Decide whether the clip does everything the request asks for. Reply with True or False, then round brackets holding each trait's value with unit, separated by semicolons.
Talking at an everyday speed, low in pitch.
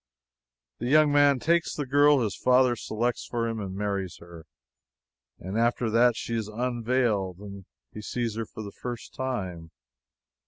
True (155 wpm; 115 Hz)